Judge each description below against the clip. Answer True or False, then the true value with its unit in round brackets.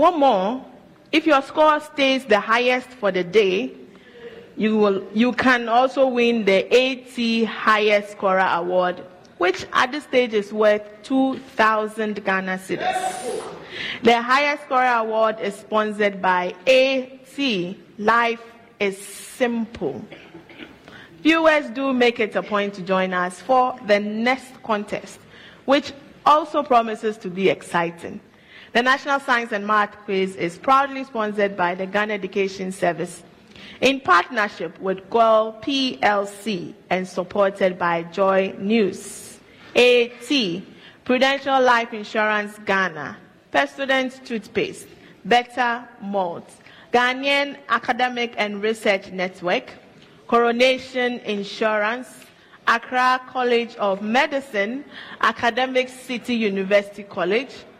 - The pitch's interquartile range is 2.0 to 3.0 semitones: False (4.1 semitones)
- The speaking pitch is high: True (220 Hz)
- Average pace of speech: False (115 wpm)